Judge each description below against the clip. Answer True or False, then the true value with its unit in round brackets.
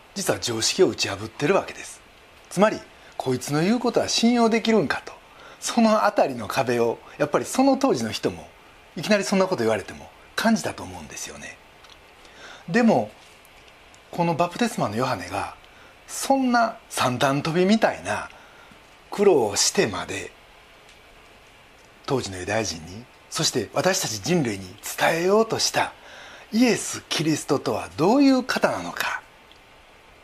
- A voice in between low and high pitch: True (175 Hz)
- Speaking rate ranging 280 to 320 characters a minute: True (300 characters per minute)